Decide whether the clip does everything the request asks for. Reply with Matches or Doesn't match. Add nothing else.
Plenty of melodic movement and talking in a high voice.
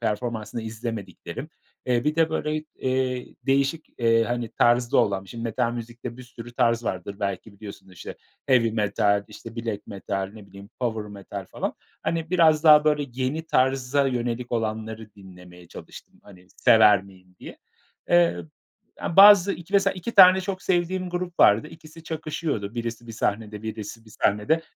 Doesn't match